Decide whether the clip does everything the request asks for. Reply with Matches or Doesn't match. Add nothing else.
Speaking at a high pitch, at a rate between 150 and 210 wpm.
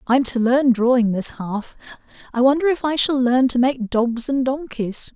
Matches